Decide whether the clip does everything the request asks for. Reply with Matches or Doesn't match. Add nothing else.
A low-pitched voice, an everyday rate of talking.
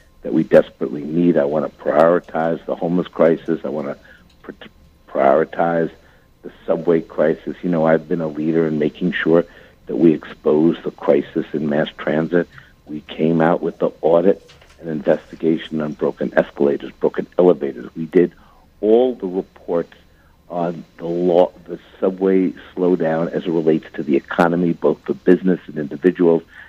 Matches